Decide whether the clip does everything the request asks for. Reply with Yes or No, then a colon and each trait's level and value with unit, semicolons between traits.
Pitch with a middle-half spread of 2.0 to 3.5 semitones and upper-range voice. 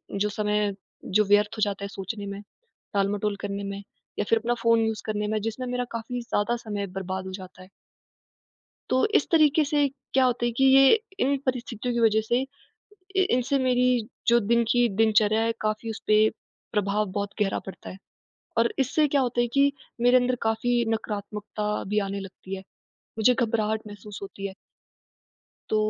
Yes: average, 2.9 semitones; high, 220 Hz